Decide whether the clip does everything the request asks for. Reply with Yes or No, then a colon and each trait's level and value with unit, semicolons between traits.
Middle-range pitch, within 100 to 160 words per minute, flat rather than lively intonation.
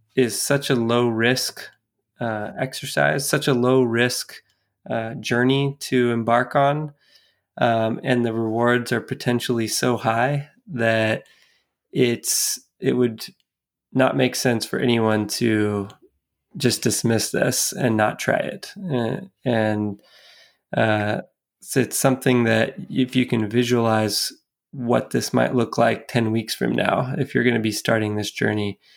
No: low, 120 Hz; average, 140 wpm; narrow, 2.3 semitones